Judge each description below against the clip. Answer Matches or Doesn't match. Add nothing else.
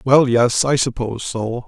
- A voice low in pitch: Matches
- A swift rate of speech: Doesn't match